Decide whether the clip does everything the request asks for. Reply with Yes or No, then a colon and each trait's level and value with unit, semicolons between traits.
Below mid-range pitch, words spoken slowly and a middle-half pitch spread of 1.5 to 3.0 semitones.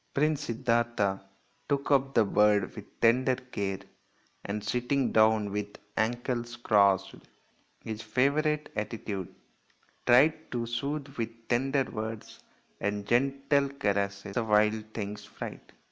No: low, 115 Hz; slow, 115 wpm; average, 4.2 semitones